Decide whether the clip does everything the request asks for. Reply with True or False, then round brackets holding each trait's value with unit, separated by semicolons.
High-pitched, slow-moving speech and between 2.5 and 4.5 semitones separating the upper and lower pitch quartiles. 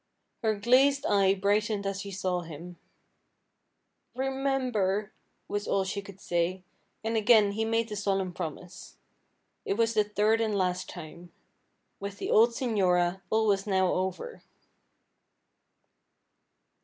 True (200 Hz; 130 wpm; 2.9 semitones)